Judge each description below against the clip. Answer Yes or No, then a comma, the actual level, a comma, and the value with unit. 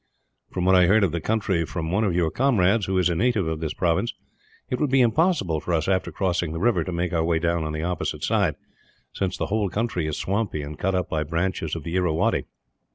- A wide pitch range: No, average, 3.6 semitones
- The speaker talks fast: Yes, fast, 240 wpm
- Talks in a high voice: No, very low, 90 Hz